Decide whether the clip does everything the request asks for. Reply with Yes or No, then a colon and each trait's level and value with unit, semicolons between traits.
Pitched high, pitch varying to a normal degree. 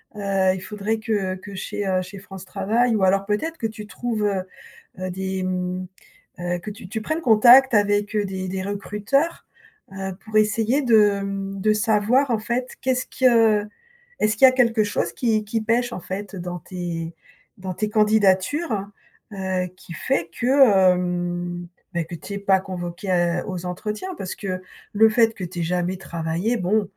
Yes: high, 200 Hz; average, 3.0 semitones